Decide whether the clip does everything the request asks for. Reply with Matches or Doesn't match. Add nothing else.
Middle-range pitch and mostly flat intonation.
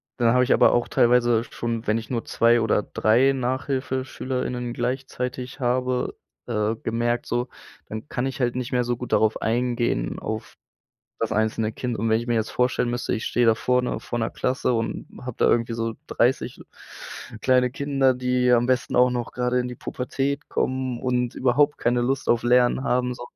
Doesn't match